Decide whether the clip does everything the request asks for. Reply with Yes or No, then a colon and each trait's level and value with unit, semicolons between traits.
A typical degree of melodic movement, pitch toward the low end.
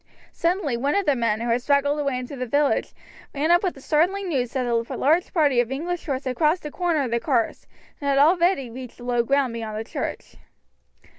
No: average, 4.4 semitones; very high, 275 Hz